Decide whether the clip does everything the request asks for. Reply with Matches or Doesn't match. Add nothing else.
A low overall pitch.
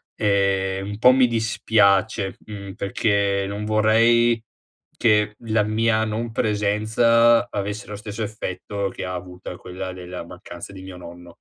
Matches